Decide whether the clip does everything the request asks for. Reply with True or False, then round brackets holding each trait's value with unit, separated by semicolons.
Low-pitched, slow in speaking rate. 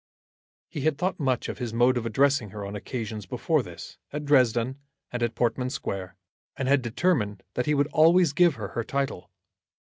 False (125 Hz; 185 wpm)